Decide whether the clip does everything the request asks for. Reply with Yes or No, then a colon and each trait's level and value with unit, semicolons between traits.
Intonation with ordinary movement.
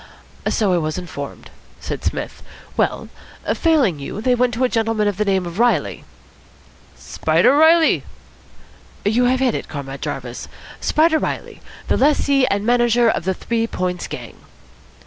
No: wide, 5.8 semitones